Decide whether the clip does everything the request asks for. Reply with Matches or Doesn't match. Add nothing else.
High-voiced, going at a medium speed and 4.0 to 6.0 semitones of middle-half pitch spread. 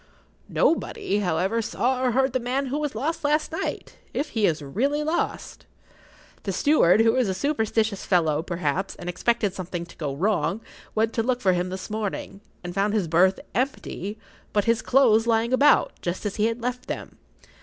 Matches